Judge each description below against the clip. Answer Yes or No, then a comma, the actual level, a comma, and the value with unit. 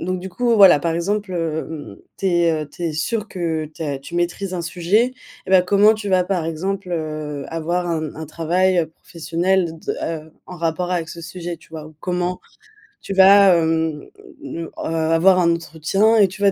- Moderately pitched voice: Yes, medium, 175 Hz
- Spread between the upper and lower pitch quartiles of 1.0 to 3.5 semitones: Yes, average, 2.8 semitones